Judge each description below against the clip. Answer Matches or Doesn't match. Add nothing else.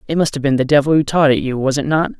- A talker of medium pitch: Matches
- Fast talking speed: Matches